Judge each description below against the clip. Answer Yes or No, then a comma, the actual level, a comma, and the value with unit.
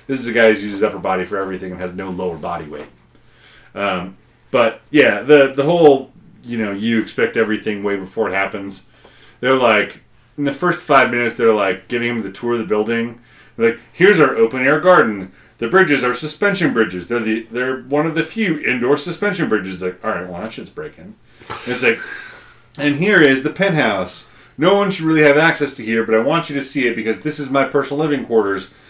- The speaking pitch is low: Yes, low, 120 Hz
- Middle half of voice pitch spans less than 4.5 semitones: No, average, 5.1 semitones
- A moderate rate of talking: No, fast, 220 wpm